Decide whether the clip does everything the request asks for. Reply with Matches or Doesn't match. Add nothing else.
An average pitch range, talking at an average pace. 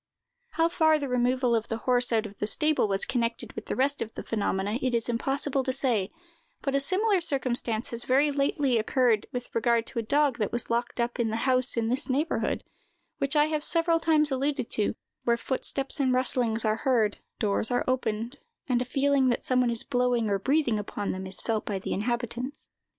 Doesn't match